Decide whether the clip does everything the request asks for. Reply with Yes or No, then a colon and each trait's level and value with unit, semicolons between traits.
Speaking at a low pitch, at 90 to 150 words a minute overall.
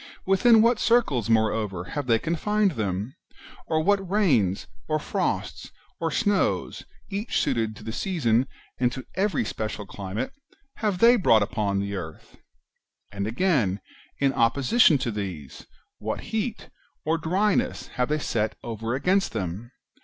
Yes: low, 130 Hz; average, 140 wpm